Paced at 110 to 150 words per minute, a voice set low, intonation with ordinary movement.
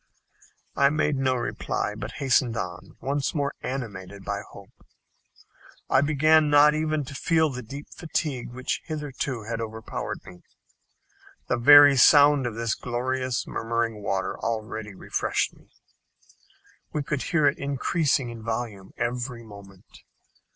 Yes: slow, 135 wpm; low, 125 Hz; average, 4.4 semitones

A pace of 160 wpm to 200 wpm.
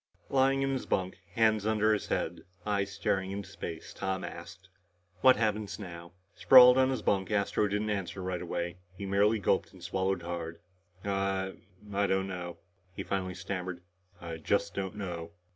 Yes: average, 165 wpm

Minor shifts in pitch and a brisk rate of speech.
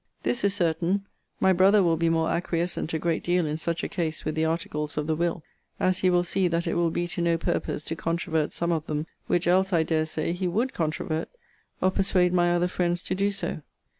Yes: narrow, 2.0 semitones; fast, 230 wpm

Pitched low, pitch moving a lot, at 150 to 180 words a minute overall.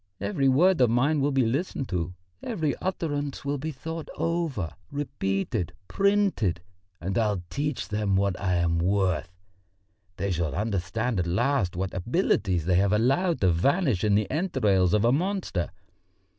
Yes: low, 110 Hz; wide, 7.8 semitones; average, 155 wpm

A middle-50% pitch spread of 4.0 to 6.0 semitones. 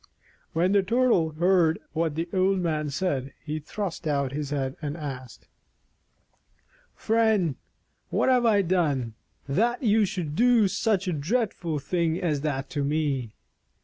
Yes: average, 5.3 semitones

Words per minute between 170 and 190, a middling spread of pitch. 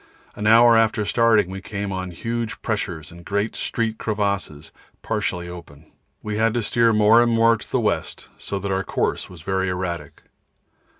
Yes: average, 175 wpm; average, 3.7 semitones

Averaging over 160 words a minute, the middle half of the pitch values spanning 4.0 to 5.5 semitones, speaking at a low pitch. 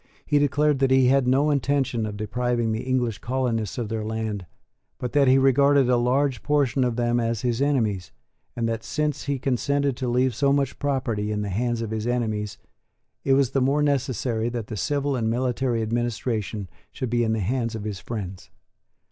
No: average, 195 wpm; average, 3.3 semitones; low, 120 Hz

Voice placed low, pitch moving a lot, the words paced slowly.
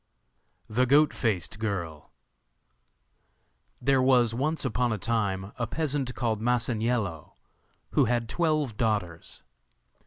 No: low, 115 Hz; average, 3.5 semitones; slow, 105 wpm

